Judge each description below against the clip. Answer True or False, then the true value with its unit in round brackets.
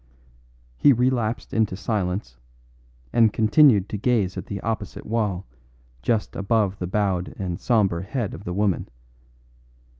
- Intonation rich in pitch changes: False (3.3 semitones)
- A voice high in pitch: False (105 Hz)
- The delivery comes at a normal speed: False (130 wpm)